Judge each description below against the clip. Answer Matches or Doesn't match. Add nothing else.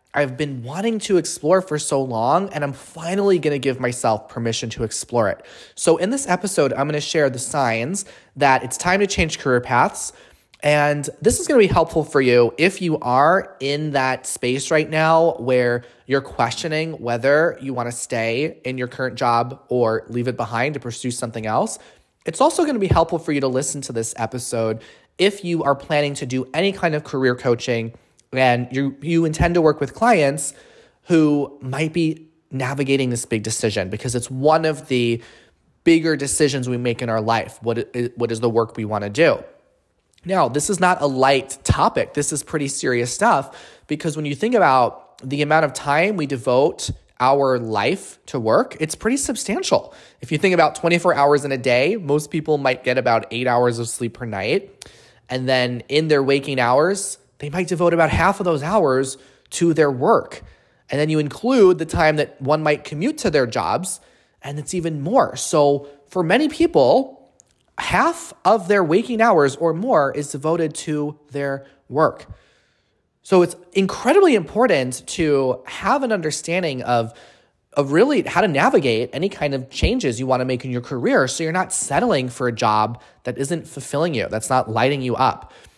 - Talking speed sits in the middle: Matches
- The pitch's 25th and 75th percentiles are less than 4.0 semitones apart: Doesn't match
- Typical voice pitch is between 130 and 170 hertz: Matches